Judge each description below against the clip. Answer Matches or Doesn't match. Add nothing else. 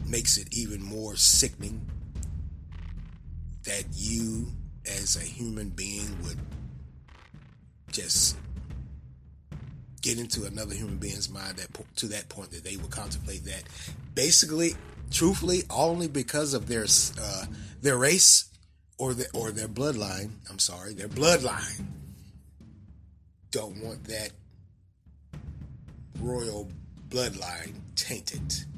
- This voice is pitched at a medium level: Doesn't match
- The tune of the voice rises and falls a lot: Matches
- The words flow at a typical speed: Doesn't match